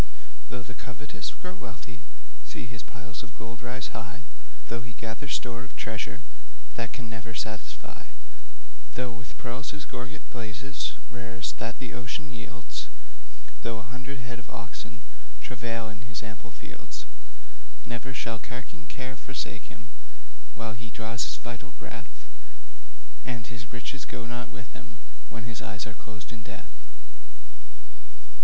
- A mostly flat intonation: Yes, narrow, 2.0 semitones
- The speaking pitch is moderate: No, low, 120 Hz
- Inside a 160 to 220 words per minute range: No, average, 150 wpm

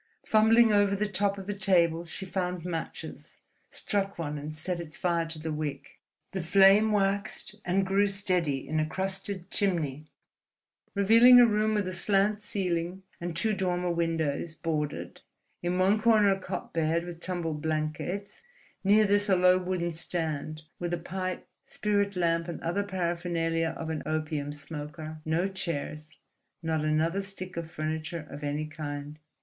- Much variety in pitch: No, average, 3.7 semitones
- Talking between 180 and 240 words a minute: No, average, 155 wpm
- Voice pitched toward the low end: No, medium, 175 Hz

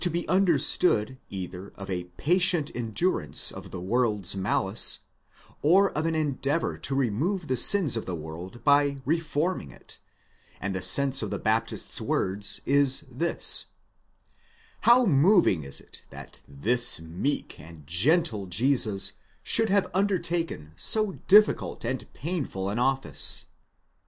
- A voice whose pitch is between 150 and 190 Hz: No, low, 135 Hz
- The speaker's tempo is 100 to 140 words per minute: Yes, slow, 135 wpm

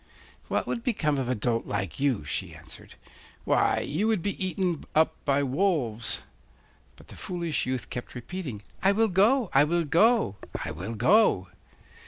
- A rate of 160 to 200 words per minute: Yes, average, 165 wpm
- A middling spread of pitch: No, wide, 7.9 semitones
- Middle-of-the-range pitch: Yes, medium, 155 Hz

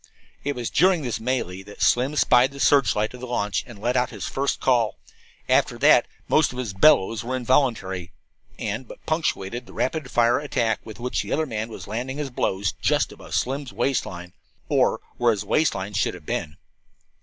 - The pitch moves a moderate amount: Yes, average, 4.3 semitones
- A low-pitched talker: Yes, low, 120 Hz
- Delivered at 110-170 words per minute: No, average, 195 wpm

